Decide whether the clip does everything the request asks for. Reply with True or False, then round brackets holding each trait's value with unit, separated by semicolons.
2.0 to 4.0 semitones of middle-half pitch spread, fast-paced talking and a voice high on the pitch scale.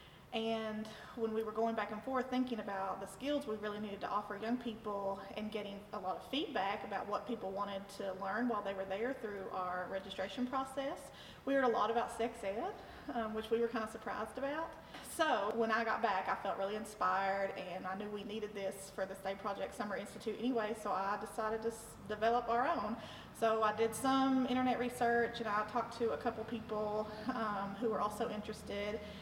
True (2.6 semitones; 210 wpm; 215 Hz)